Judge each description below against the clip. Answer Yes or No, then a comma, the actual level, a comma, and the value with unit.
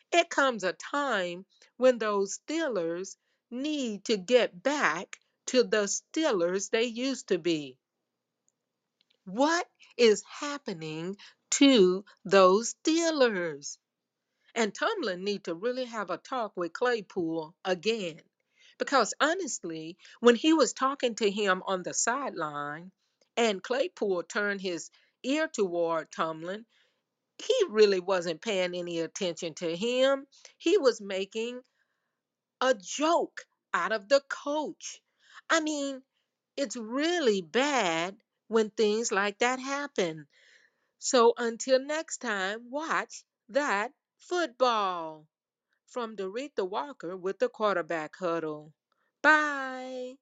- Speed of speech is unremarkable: No, slow, 115 wpm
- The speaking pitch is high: Yes, high, 225 Hz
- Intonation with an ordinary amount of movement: No, wide, 6.6 semitones